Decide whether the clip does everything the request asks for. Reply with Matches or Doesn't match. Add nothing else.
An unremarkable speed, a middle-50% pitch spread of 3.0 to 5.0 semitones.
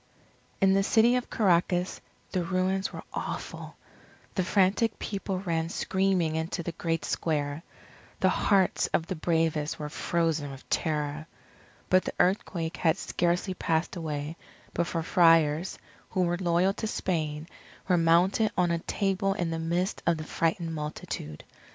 Doesn't match